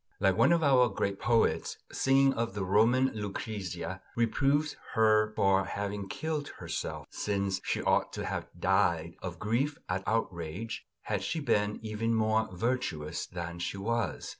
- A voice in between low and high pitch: No, low, 105 Hz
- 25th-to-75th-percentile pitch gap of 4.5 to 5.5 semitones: No, average, 3.7 semitones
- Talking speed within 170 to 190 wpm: No, average, 160 wpm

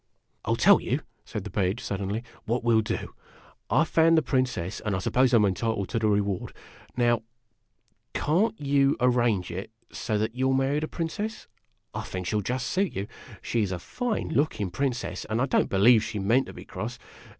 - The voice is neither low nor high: No, low, 115 Hz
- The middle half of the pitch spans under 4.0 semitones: No, average, 5.0 semitones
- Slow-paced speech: No, fast, 205 wpm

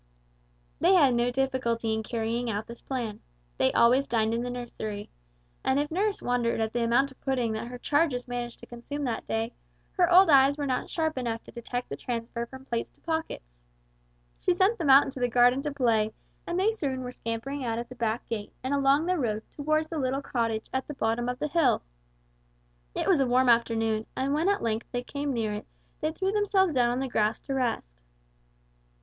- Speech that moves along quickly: Yes, fast, 210 wpm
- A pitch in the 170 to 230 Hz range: No, very high, 250 Hz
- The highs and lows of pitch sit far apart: No, average, 3.7 semitones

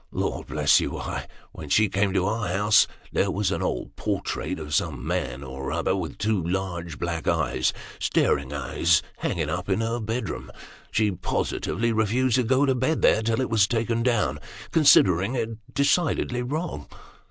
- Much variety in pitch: Yes, wide, 5.7 semitones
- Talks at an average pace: Yes, average, 165 wpm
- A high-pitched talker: No, low, 110 Hz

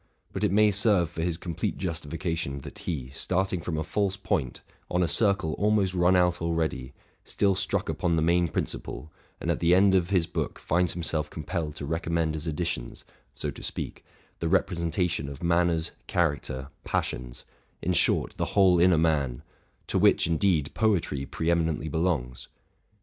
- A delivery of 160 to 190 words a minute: Yes, average, 170 wpm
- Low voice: Yes, very low, 85 Hz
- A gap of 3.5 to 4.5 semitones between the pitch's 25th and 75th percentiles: No, average, 2.7 semitones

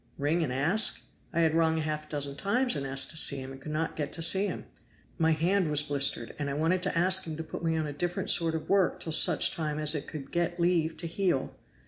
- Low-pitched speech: No, medium, 160 Hz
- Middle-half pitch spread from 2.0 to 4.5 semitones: Yes, average, 2.7 semitones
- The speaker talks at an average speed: No, fast, 260 wpm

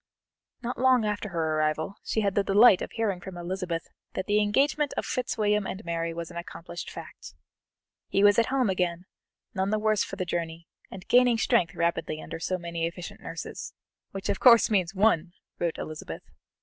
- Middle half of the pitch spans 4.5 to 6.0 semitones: No, average, 3.9 semitones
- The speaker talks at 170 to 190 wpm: Yes, average, 185 wpm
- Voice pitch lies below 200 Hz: Yes, high, 190 Hz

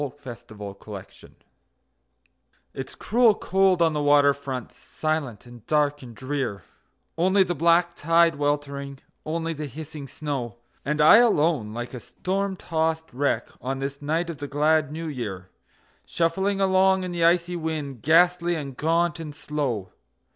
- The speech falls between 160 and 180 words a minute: No, average, 150 wpm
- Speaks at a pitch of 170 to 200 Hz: No, medium, 150 Hz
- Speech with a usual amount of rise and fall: Yes, average, 3.8 semitones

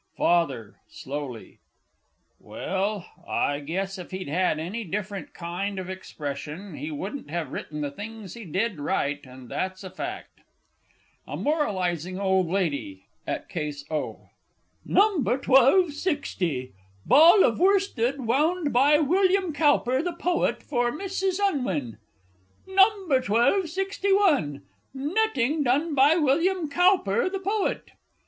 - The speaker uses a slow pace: Yes, slow, 120 wpm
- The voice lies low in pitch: No, high, 230 Hz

